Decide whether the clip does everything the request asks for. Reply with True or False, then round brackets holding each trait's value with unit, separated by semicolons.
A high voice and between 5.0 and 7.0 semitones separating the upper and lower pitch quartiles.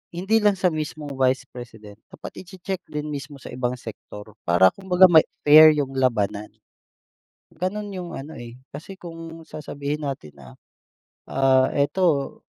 False (145 Hz; 5.4 semitones)